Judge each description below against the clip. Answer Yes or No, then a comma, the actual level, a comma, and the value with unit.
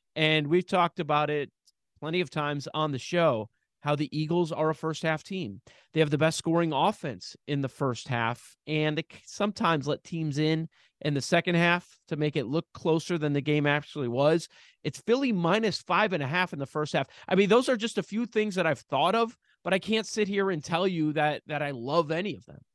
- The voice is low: No, medium, 160 Hz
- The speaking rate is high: Yes, fast, 230 wpm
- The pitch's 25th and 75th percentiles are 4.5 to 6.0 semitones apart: No, average, 3.4 semitones